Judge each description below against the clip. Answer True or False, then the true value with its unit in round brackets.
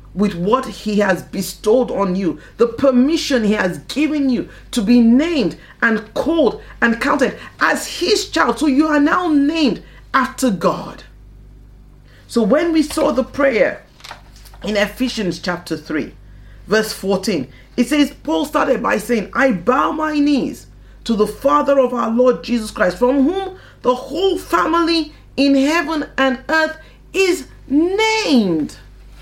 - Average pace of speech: True (145 wpm)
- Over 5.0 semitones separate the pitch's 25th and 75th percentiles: True (5.5 semitones)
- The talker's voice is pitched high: True (265 Hz)